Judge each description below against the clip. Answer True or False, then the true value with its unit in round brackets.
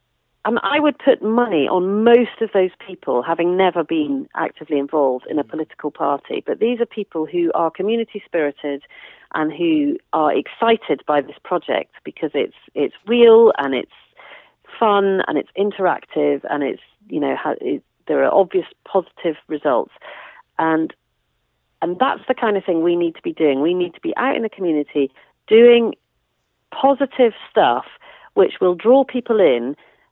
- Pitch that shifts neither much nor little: False (6.7 semitones)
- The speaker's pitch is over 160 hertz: True (185 Hz)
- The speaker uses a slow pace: False (165 wpm)